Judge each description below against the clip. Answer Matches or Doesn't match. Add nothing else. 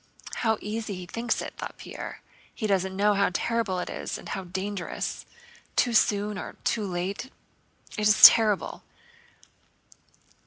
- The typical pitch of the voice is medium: Doesn't match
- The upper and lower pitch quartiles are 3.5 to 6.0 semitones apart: Doesn't match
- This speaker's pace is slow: Doesn't match